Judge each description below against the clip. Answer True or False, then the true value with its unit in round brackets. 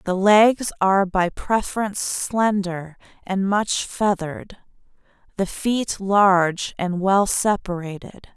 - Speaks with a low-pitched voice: False (195 Hz)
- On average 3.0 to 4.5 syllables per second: True (3.7 syllables/s)